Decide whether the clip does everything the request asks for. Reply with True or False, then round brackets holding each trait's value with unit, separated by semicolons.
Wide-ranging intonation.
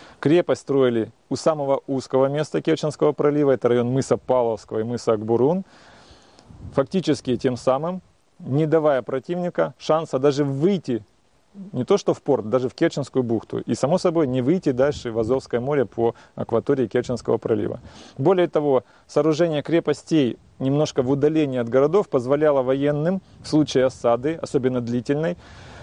False (3.9 semitones)